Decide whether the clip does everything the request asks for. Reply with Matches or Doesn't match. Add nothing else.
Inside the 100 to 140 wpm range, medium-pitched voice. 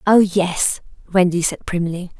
Matches